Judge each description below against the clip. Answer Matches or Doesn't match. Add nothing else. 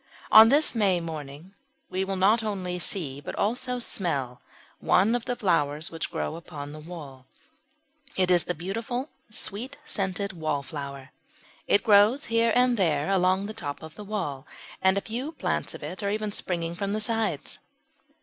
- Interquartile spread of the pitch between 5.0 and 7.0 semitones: Matches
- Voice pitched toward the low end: Doesn't match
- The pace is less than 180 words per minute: Matches